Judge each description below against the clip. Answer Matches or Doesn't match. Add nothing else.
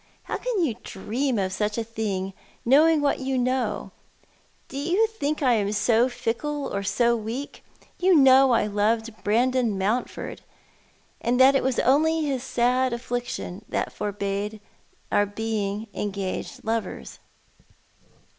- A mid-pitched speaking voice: Doesn't match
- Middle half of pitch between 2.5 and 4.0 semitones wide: Doesn't match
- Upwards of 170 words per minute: Doesn't match